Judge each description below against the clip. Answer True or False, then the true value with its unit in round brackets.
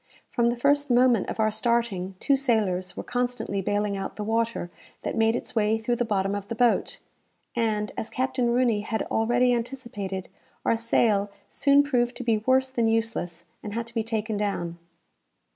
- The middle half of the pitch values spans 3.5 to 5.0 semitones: False (2.8 semitones)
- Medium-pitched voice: False (225 Hz)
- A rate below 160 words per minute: False (180 wpm)